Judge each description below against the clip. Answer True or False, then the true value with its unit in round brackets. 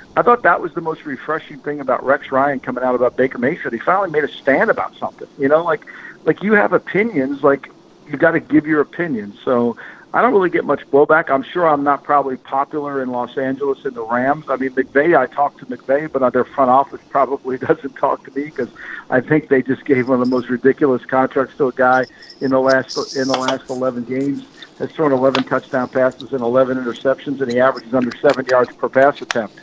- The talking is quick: True (225 wpm)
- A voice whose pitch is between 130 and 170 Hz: True (135 Hz)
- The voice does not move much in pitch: True (2.0 semitones)